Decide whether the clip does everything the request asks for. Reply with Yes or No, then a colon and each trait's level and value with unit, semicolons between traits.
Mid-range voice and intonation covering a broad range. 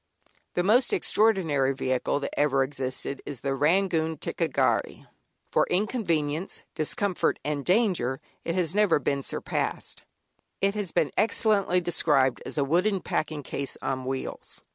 Yes: medium, 160 Hz; wide, 5.8 semitones